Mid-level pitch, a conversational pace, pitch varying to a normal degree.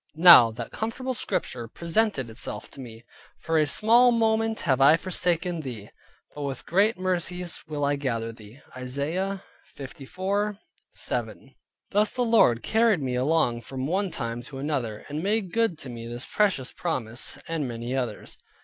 No: medium, 155 Hz; average, 155 wpm; wide, 7.6 semitones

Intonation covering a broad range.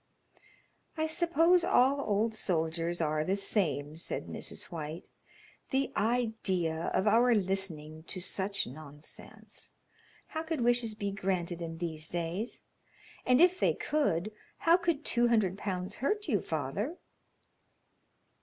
Yes: wide, 7.0 semitones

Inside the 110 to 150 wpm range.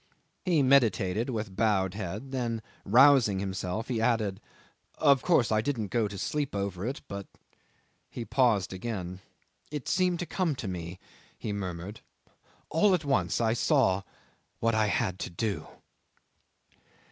Yes: average, 145 wpm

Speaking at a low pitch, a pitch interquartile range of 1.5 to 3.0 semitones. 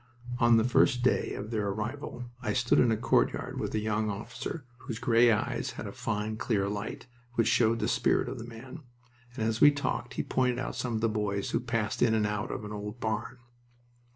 Yes: low, 115 Hz; narrow, 2.4 semitones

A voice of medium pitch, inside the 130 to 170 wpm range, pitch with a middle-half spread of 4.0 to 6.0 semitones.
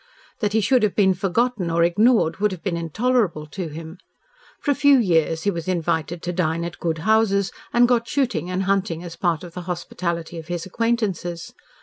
No: medium, 180 Hz; average, 200 wpm; average, 4.3 semitones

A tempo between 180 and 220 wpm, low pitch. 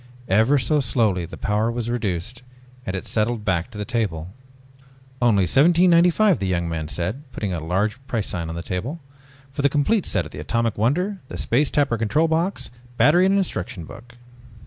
Yes: average, 185 wpm; low, 115 Hz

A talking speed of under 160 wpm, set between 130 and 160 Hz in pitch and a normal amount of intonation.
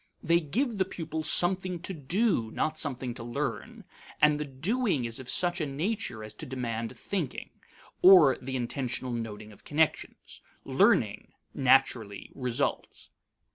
No: average, 140 wpm; medium, 140 Hz; wide, 6.3 semitones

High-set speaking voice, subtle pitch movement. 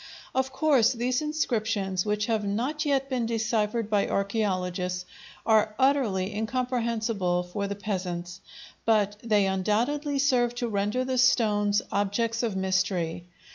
No: high, 215 Hz; average, 3.8 semitones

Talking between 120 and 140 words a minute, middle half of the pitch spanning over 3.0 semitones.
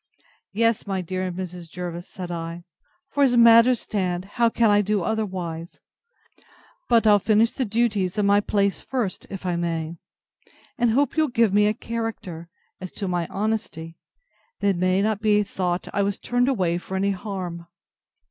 No: average, 165 wpm; average, 3.9 semitones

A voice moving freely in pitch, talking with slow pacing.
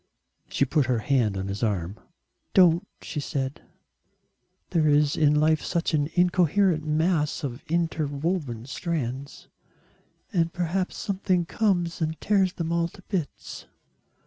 No: average, 3.9 semitones; slow, 130 wpm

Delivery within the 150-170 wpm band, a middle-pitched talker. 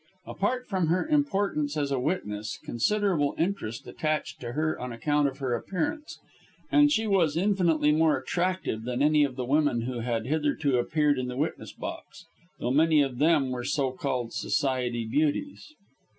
Yes: average, 165 wpm; medium, 150 Hz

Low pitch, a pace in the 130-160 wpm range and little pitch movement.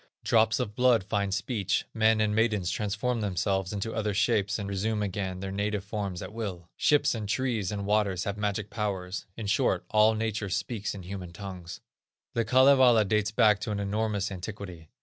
No: low, 105 Hz; average, 180 wpm; narrow, 2.1 semitones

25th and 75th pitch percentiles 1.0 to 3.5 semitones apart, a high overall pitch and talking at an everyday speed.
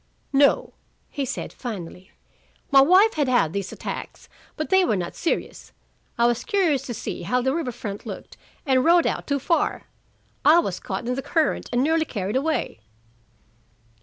No: wide, 5.4 semitones; very high, 270 Hz; average, 170 wpm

